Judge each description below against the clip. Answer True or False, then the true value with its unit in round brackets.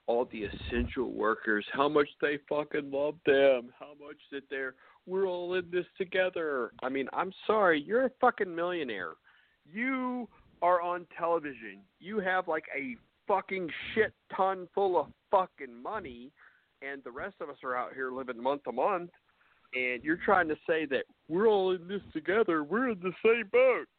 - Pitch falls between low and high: True (180 Hz)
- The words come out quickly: False (175 wpm)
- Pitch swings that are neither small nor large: False (7.0 semitones)